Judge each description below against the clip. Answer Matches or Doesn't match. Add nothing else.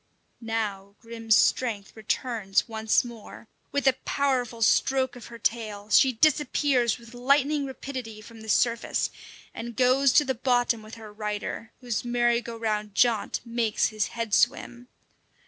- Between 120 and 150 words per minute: Matches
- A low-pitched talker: Doesn't match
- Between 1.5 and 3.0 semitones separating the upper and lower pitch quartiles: Matches